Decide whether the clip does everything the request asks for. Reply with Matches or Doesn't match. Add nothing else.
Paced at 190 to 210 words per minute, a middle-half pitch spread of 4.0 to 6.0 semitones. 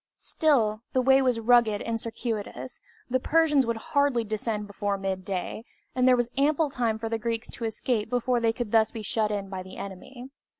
Doesn't match